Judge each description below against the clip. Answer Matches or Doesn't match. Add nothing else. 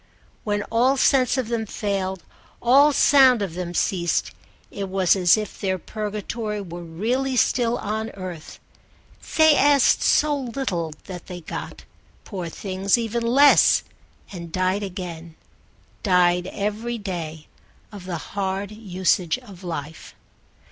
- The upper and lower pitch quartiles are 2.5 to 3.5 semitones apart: Doesn't match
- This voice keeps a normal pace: Doesn't match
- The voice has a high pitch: Matches